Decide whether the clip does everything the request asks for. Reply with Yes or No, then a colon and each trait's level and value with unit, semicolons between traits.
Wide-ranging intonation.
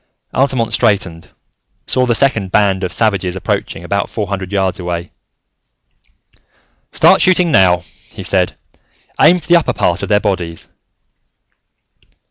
No: average, 4.5 semitones